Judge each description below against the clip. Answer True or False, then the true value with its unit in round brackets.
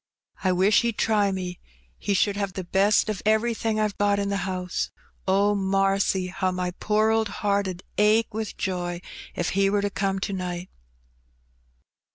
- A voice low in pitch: False (195 Hz)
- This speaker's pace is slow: False (175 wpm)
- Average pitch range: False (1.9 semitones)